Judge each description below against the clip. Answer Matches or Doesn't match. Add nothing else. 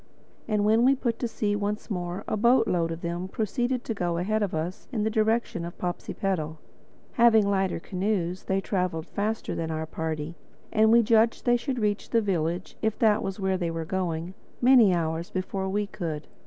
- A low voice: Doesn't match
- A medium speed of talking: Matches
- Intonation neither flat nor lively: Matches